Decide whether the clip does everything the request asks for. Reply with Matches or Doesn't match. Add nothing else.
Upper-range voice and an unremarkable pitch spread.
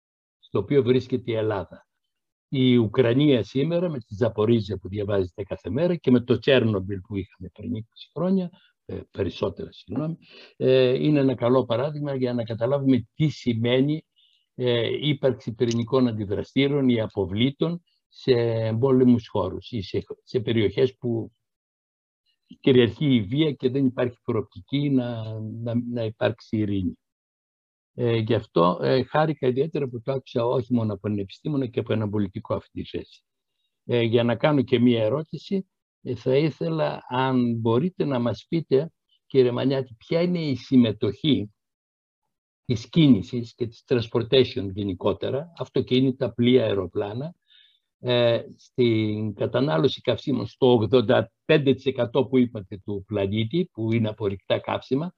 Doesn't match